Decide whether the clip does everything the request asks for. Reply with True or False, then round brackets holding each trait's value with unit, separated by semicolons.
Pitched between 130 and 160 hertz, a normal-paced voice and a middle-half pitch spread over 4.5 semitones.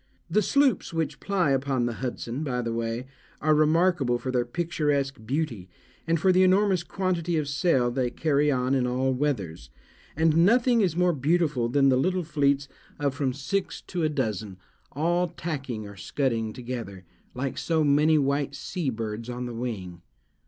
True (140 Hz; 170 wpm; 5.1 semitones)